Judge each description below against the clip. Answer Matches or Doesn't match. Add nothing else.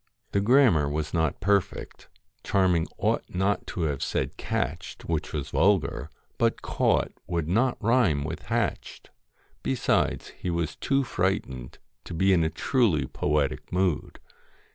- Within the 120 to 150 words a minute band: Matches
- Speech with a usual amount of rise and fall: Matches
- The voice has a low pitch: Matches